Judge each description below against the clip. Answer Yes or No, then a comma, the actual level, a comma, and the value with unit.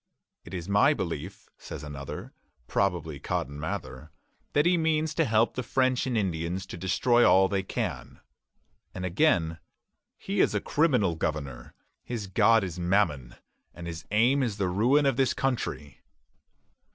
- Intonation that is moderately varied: No, wide, 7.0 semitones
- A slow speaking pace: No, average, 150 wpm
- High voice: No, very low, 95 Hz